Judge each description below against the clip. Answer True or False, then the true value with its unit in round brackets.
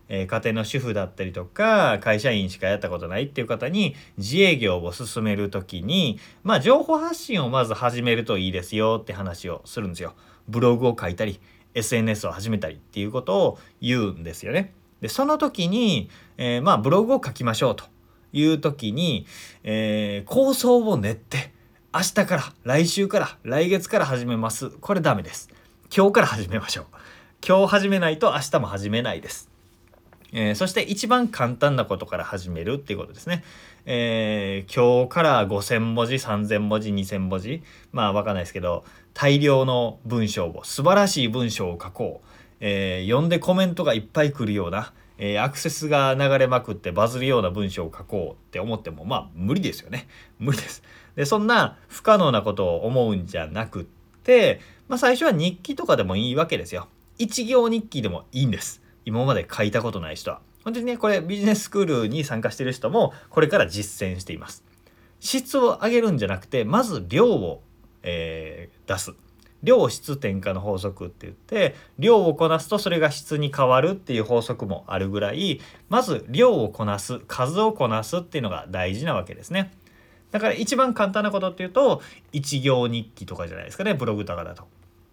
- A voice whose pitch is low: True (120 Hz)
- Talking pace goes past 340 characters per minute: True (350 characters per minute)